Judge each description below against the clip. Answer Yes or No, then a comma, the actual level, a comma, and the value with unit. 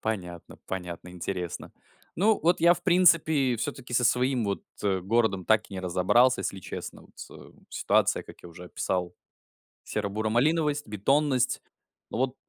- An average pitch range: No, wide, 6.9 semitones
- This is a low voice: Yes, low, 110 Hz